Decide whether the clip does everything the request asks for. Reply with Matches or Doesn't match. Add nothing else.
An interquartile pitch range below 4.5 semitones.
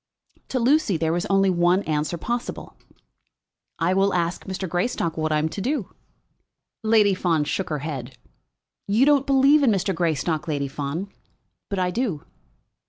Doesn't match